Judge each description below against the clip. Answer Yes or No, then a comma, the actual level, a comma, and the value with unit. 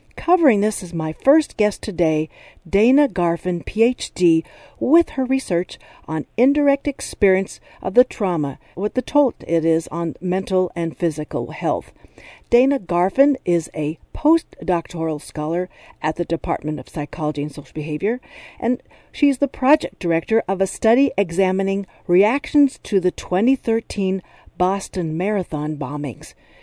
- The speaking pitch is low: No, medium, 185 Hz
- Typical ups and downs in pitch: No, wide, 6.9 semitones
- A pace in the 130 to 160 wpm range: Yes, slow, 135 wpm